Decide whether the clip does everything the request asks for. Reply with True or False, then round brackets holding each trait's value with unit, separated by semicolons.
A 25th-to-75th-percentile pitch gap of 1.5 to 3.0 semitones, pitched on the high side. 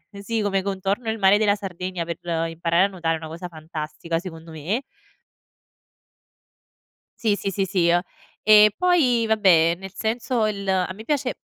False (4.1 semitones; 195 Hz)